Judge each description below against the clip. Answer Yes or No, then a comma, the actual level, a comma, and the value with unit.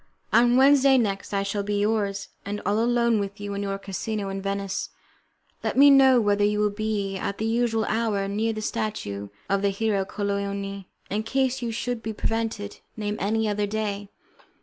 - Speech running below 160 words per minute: No, average, 185 wpm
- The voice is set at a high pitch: Yes, high, 210 Hz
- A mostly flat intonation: Yes, narrow, 2.1 semitones